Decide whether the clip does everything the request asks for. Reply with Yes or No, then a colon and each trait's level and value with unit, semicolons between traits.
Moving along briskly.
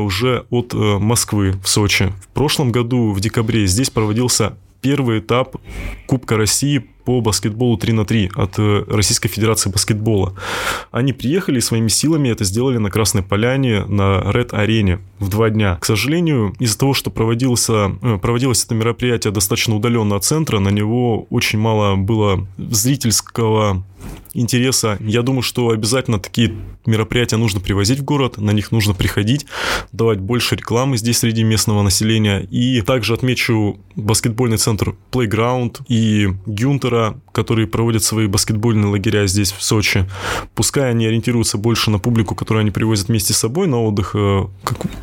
No: average, 150 wpm